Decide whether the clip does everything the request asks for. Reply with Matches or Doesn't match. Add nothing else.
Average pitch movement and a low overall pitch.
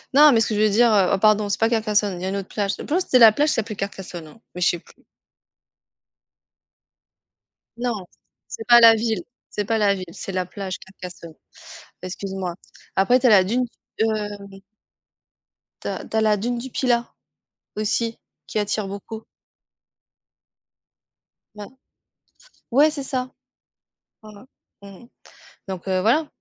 Doesn't match